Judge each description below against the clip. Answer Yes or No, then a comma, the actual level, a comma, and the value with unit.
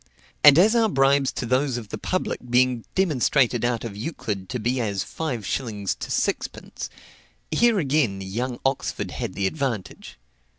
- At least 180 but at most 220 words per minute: No, average, 160 wpm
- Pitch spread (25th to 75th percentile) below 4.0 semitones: No, average, 4.5 semitones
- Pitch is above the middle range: No, low, 125 Hz